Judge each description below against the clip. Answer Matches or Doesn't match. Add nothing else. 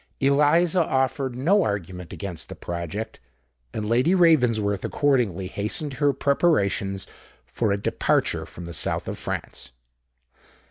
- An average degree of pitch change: Doesn't match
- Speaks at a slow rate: Matches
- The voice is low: Matches